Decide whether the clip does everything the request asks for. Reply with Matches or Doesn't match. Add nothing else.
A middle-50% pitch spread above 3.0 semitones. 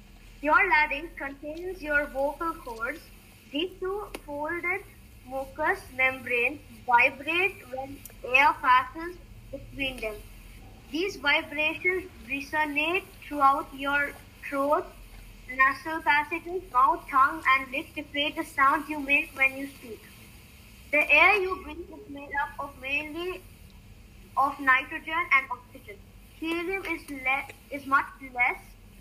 Matches